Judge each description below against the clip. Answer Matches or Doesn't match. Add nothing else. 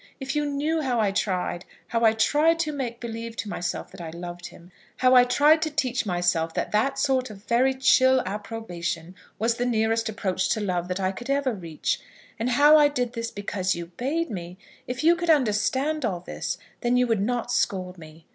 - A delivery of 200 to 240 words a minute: Matches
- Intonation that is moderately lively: Doesn't match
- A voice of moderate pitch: Doesn't match